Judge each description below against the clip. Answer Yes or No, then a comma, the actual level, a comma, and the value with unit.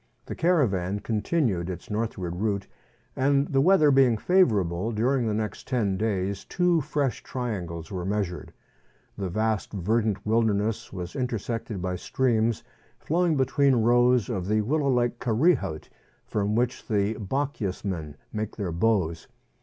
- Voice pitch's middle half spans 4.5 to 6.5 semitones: Yes, average, 4.8 semitones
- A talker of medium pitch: No, low, 110 Hz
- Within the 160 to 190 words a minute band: No, average, 140 wpm